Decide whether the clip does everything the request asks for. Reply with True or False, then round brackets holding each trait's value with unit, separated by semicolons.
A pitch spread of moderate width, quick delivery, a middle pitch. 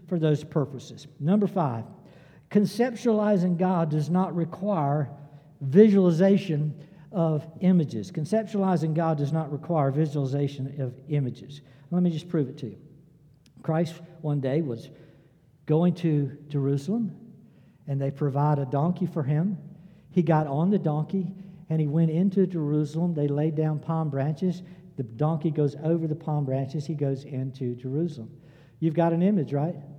False (3.3 semitones; 145 wpm; 155 Hz)